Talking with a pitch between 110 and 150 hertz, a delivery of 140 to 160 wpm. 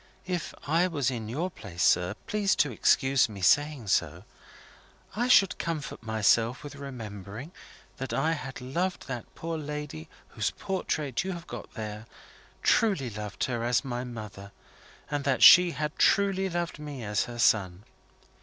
Yes: low, 135 Hz; average, 155 wpm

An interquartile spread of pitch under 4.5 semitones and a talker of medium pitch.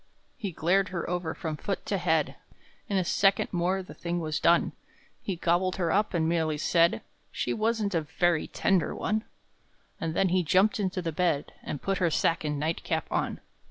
Yes: average, 2.9 semitones; medium, 175 Hz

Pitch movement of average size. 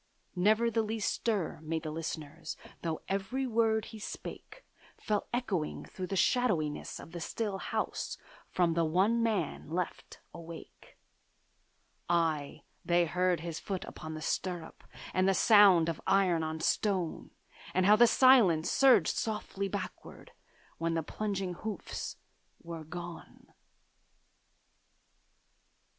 Yes: average, 4.5 semitones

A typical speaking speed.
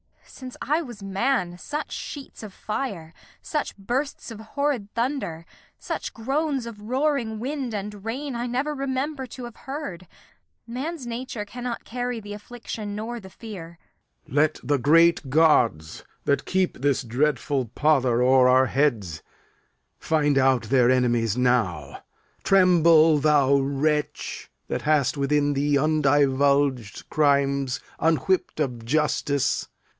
No: slow, 130 wpm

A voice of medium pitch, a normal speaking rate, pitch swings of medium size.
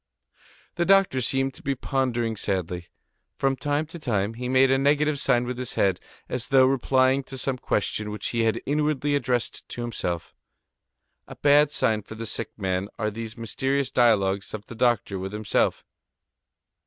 No: low, 125 Hz; average, 170 wpm; average, 4.0 semitones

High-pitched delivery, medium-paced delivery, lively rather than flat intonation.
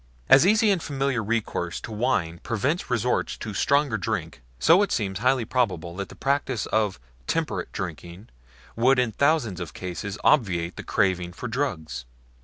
No: low, 110 Hz; average, 160 wpm; wide, 6.6 semitones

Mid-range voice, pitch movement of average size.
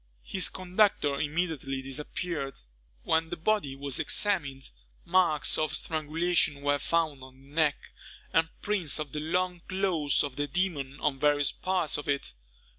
Yes: medium, 155 Hz; average, 3.9 semitones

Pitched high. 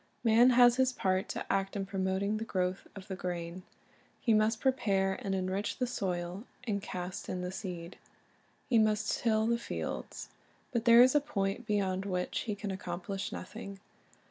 Yes: high, 200 Hz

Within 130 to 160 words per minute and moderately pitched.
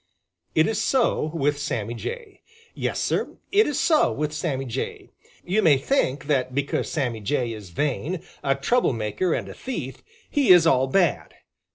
No: average, 170 wpm; medium, 150 Hz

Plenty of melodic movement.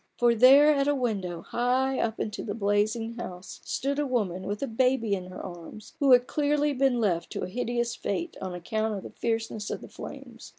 No: average, 4.4 semitones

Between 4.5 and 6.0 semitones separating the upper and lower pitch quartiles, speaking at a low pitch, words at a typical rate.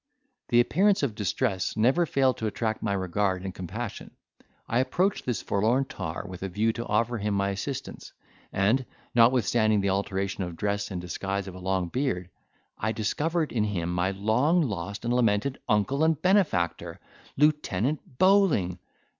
Yes: average, 5.2 semitones; low, 105 Hz; average, 160 wpm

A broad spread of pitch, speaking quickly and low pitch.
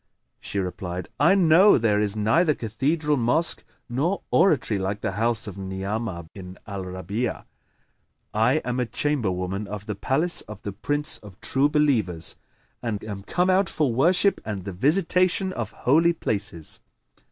No: wide, 7.3 semitones; average, 150 wpm; low, 115 Hz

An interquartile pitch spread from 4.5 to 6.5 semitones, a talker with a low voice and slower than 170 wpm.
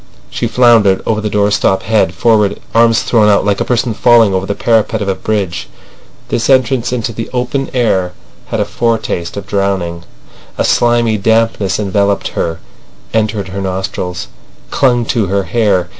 No: average, 3.1 semitones; low, 105 Hz; average, 160 wpm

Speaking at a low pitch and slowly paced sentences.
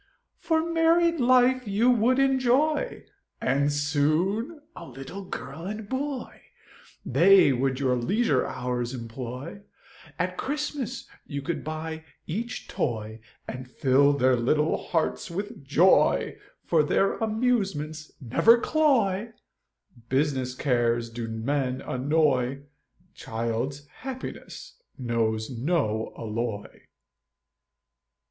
No: medium, 150 Hz; slow, 100 wpm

